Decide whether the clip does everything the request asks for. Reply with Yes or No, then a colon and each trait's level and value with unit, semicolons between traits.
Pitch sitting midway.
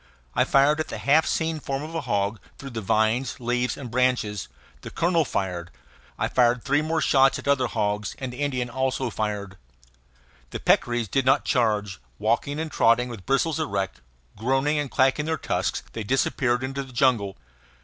No: low, 125 Hz